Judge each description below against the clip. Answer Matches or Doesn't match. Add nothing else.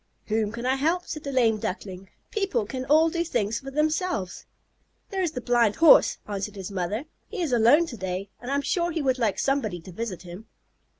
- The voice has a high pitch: Matches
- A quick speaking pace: Matches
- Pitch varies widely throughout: Matches